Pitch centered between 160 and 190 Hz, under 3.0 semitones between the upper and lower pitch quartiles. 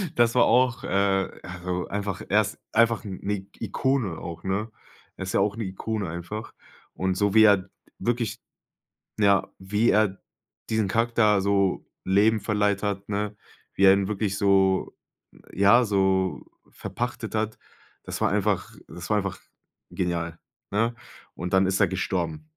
No: low, 100 Hz; narrow, 2.4 semitones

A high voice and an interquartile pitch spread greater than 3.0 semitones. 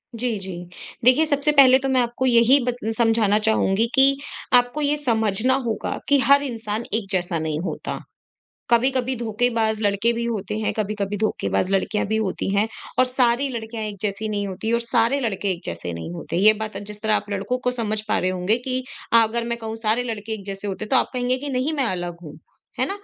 Yes: high, 225 Hz; average, 3.5 semitones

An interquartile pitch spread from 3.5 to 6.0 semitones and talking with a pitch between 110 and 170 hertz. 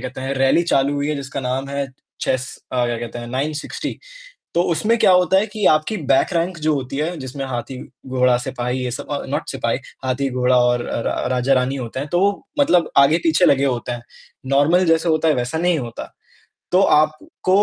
Yes: average, 4.3 semitones; medium, 140 Hz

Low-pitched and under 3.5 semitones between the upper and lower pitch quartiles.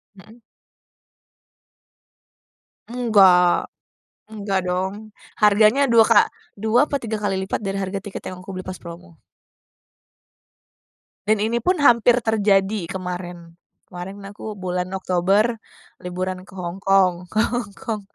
No: high, 195 Hz; average, 3.0 semitones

